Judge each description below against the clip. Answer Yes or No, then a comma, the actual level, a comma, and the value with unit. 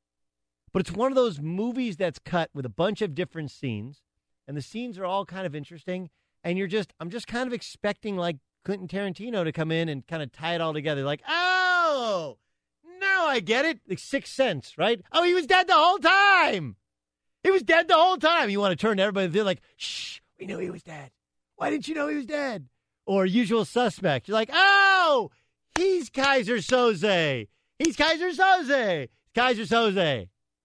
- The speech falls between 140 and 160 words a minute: No, average, 200 wpm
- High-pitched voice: Yes, high, 200 Hz